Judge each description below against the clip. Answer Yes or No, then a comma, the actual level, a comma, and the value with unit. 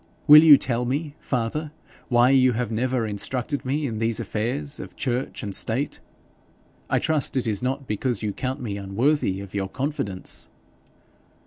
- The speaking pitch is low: Yes, low, 125 Hz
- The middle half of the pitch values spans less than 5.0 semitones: Yes, average, 4.1 semitones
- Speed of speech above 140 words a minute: Yes, average, 160 wpm